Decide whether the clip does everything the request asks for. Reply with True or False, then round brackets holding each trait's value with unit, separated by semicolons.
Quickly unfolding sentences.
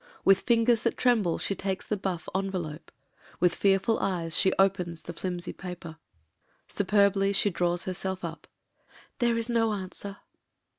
False (160 wpm)